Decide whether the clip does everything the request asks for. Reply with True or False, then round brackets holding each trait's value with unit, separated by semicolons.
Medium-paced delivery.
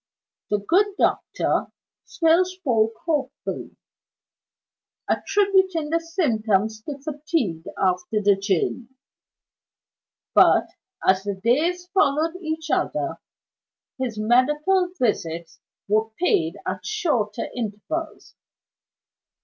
False (90 wpm)